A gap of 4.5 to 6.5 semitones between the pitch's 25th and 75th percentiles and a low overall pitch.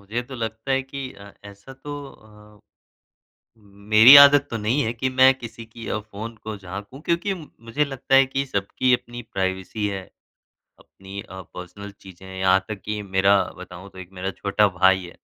Yes: average, 4.8 semitones; low, 110 Hz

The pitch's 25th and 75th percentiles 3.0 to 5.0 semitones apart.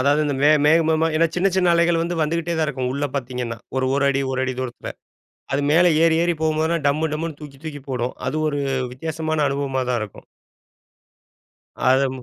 Yes: average, 3.4 semitones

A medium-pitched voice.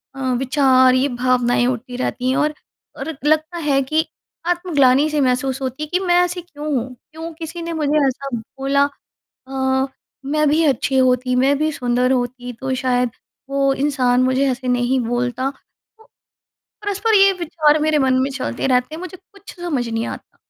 No: very high, 270 Hz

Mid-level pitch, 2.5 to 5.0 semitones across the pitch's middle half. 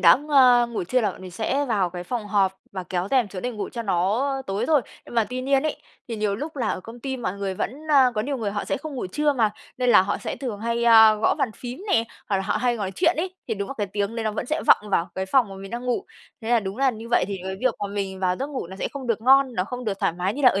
No: high, 225 Hz; average, 4.5 semitones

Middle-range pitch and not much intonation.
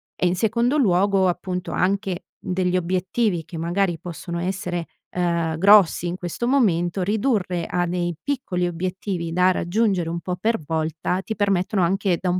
Yes: medium, 180 Hz; narrow, 2.3 semitones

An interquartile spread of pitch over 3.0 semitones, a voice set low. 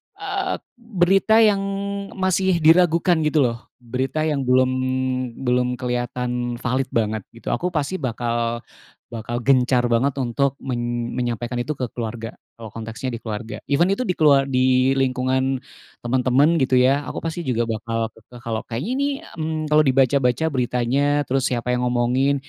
Yes: average, 3.9 semitones; low, 130 Hz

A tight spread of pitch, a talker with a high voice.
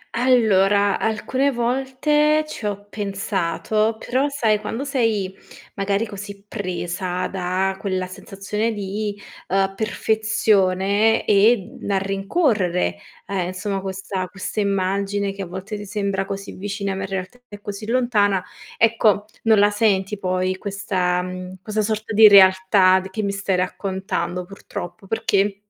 Yes: narrow, 2.3 semitones; high, 200 Hz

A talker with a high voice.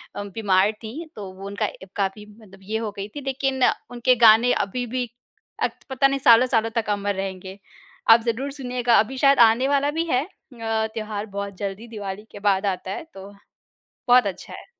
Yes: high, 220 Hz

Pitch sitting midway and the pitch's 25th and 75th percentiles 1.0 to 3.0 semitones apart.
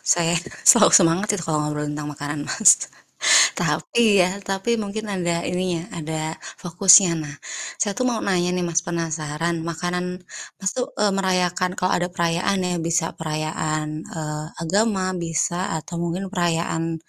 Yes: medium, 175 Hz; average, 2.7 semitones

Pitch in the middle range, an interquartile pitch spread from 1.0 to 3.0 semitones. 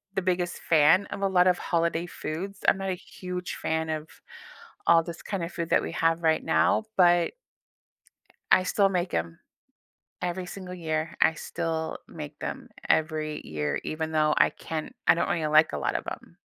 Yes: medium, 170 Hz; narrow, 2.4 semitones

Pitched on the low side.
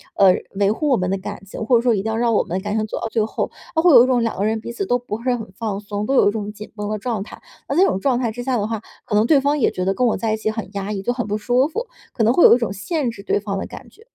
No: high, 220 Hz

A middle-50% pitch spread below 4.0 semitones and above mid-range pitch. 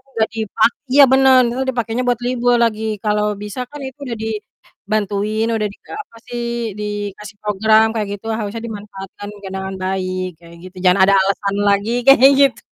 Yes: average, 2.8 semitones; high, 215 Hz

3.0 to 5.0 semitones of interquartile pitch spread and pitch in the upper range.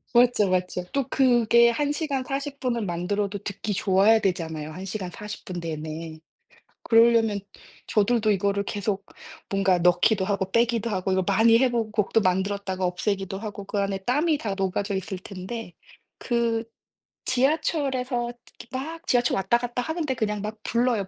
Yes: average, 4.0 semitones; high, 210 Hz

